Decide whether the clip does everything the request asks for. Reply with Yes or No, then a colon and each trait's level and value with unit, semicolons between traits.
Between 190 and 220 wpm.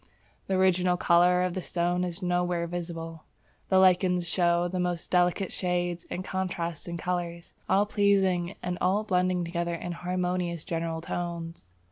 No: average, 150 wpm